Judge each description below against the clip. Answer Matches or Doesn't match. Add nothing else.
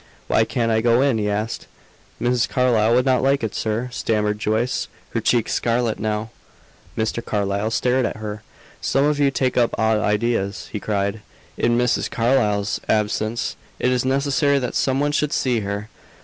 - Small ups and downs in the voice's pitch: Doesn't match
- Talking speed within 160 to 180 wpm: Matches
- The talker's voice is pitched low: Matches